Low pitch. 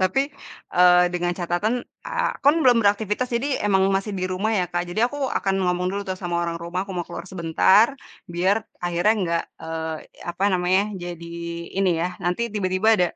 No: medium, 185 Hz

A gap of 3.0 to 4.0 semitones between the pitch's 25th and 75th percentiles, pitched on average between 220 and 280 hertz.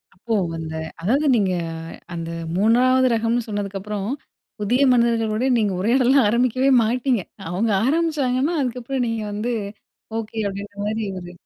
Yes: average, 3.6 semitones; high, 230 Hz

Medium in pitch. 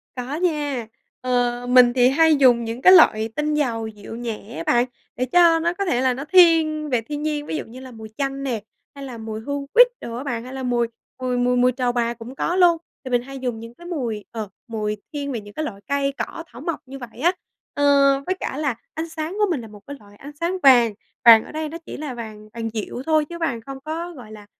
No: very high, 255 Hz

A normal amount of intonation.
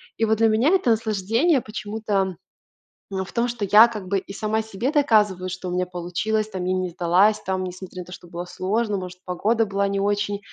Yes: average, 3.1 semitones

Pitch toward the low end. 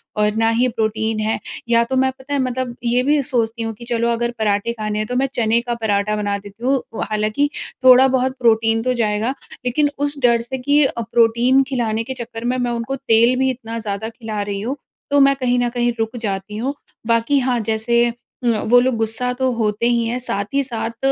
No: high, 235 Hz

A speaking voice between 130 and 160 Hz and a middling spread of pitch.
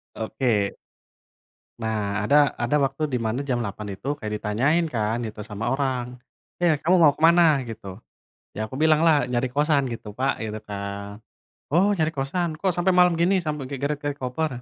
No: low, 135 Hz; wide, 5.9 semitones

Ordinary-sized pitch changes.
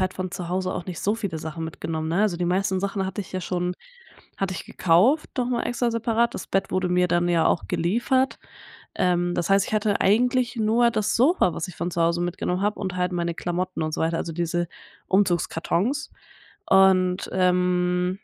Yes: average, 3.0 semitones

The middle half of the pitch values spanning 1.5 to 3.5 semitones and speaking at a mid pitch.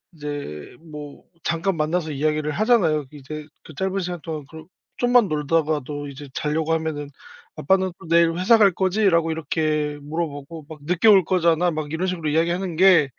Yes: average, 3.0 semitones; medium, 160 Hz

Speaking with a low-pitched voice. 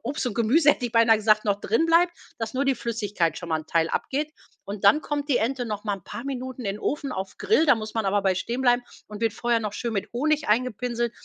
No: high, 230 Hz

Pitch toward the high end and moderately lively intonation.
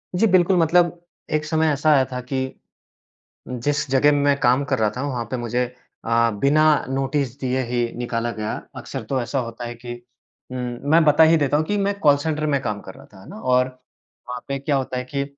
No: low, 135 Hz; average, 3.4 semitones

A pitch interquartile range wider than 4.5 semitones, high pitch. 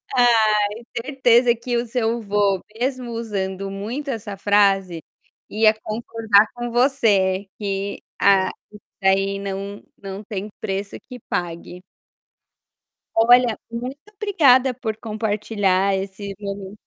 No: average, 3.3 semitones; high, 210 Hz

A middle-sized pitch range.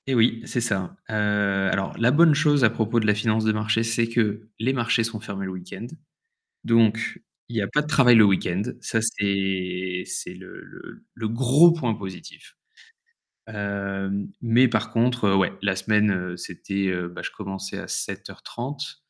Yes: average, 3.2 semitones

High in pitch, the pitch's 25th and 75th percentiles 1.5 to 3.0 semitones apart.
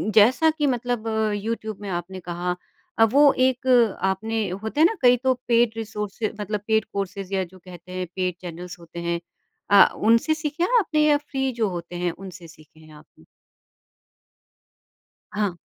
No: high, 205 Hz; average, 5.3 semitones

